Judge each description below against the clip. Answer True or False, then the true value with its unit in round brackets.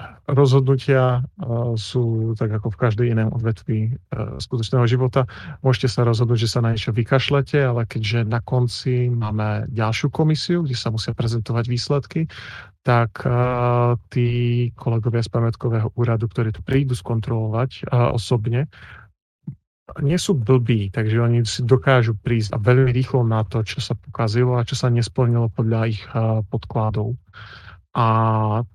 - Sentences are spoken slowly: False (140 wpm)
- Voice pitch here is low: True (120 Hz)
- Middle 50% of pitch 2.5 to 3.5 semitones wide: False (2.0 semitones)